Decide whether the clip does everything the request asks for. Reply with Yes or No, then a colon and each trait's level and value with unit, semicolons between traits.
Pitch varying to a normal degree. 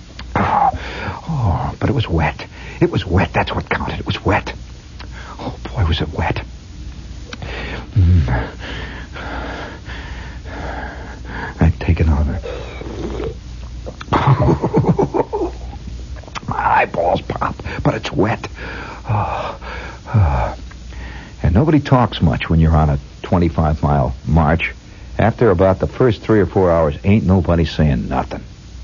Yes: average, 4.5 semitones